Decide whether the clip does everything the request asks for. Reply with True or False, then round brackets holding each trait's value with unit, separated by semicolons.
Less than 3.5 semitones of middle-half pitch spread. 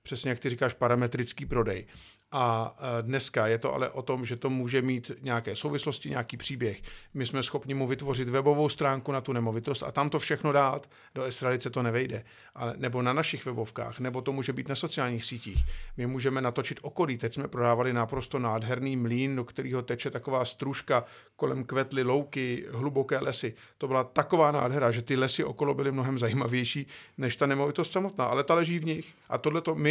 True (2.6 semitones)